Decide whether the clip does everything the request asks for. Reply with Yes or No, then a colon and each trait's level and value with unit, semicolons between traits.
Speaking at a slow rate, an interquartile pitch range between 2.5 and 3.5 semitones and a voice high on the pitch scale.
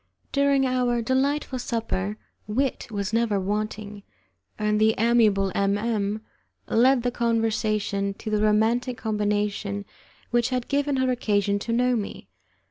Yes: slow, 130 wpm; average, 3.1 semitones; high, 220 Hz